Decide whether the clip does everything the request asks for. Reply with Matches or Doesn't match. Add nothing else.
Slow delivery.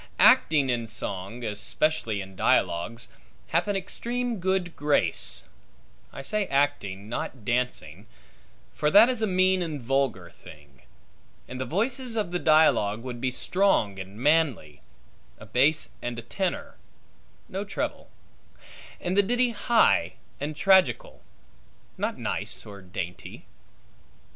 Matches